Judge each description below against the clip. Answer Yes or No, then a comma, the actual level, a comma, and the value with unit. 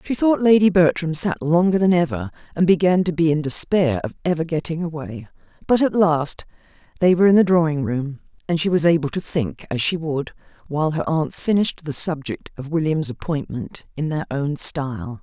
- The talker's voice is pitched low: No, medium, 160 Hz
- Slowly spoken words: No, average, 195 wpm